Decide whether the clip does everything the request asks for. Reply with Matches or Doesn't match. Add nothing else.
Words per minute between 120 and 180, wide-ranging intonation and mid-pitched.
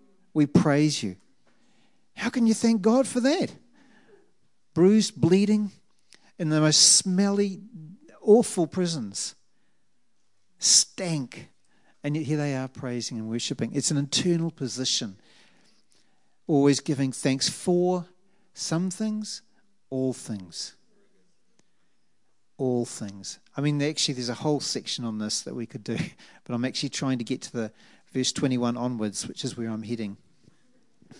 Matches